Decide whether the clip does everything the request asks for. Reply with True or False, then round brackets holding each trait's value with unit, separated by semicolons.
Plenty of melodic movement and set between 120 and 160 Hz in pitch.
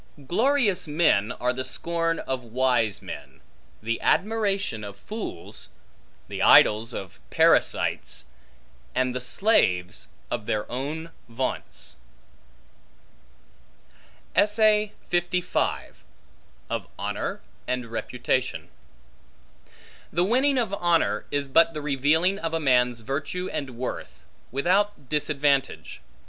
True (6.7 semitones; 140 Hz)